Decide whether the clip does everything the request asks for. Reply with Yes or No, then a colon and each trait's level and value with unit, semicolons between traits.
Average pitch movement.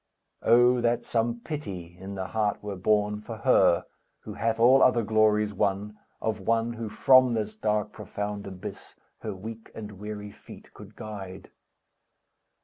No: narrow, 2.0 semitones